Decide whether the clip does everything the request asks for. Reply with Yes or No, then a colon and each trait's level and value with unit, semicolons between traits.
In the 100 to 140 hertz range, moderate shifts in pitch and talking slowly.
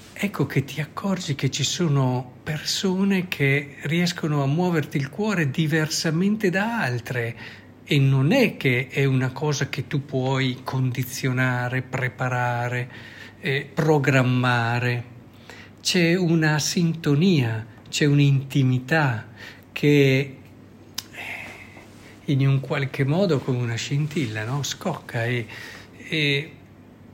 Yes: low, 135 Hz; average, 4.0 semitones; slow, 110 wpm